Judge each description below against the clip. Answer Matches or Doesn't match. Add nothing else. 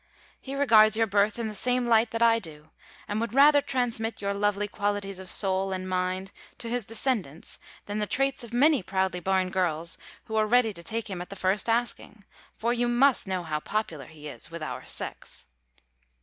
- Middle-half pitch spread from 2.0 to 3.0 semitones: Doesn't match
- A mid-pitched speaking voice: Doesn't match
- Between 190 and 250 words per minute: Matches